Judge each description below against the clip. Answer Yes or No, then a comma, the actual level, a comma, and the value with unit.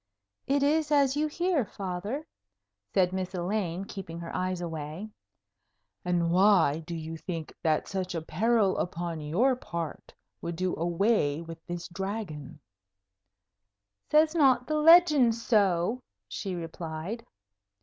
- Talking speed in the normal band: No, slow, 130 wpm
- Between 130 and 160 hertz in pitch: No, medium, 185 Hz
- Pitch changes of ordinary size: No, wide, 5.9 semitones